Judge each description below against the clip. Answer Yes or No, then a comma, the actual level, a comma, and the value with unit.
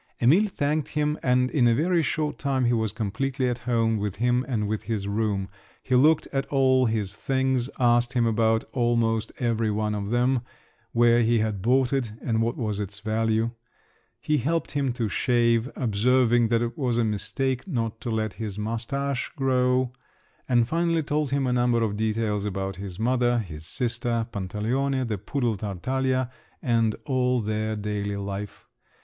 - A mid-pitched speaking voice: No, low, 120 Hz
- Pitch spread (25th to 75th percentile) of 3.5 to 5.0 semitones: No, average, 3.1 semitones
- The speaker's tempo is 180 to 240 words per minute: No, average, 170 wpm